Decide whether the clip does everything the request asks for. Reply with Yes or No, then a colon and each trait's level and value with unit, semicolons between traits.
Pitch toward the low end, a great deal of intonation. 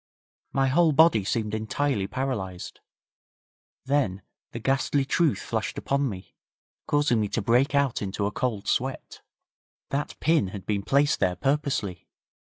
Yes: low, 125 Hz; wide, 5.7 semitones